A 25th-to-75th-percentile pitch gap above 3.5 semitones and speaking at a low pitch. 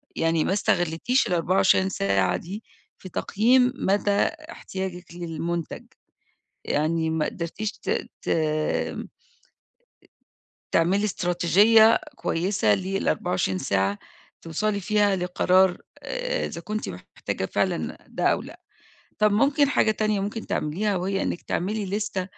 No: average, 4.1 semitones; high, 190 Hz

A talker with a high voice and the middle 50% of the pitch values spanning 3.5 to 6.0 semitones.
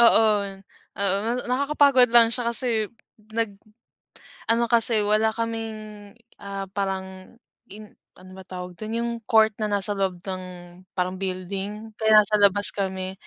No: high, 210 Hz; average, 3.0 semitones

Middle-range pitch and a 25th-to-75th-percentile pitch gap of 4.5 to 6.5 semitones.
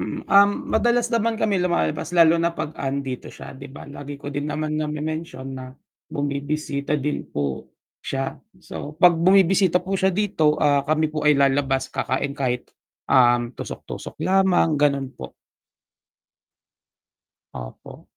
No: medium, 150 Hz; average, 4.1 semitones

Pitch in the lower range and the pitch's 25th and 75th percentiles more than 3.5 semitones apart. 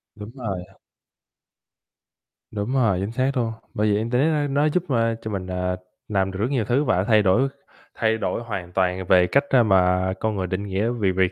Yes: low, 105 Hz; average, 4.3 semitones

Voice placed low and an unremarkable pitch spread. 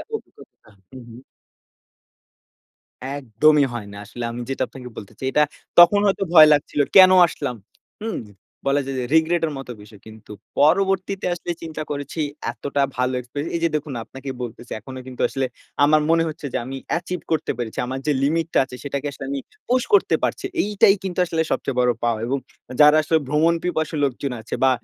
No: medium, 145 Hz; average, 4.5 semitones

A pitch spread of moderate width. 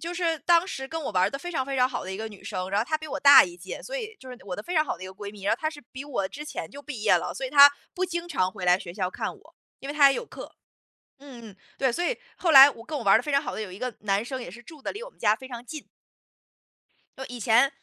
No: wide, 6.9 semitones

